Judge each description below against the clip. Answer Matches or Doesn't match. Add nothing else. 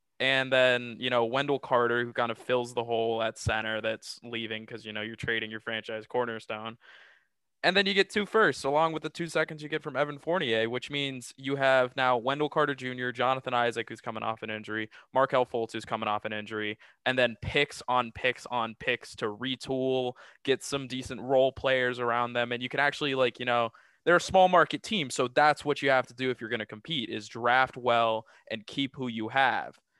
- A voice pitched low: Matches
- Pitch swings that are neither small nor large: Matches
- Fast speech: Matches